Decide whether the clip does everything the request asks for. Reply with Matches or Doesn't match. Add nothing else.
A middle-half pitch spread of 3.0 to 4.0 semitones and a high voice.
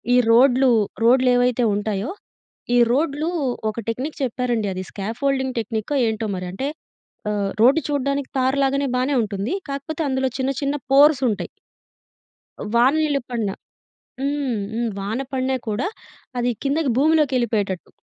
Matches